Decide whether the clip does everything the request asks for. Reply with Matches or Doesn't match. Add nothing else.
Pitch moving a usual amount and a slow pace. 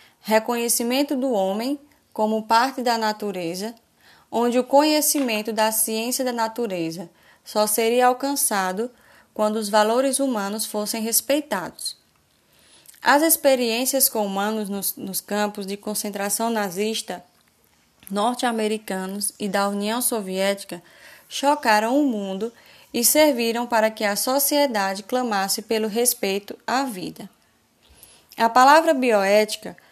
Matches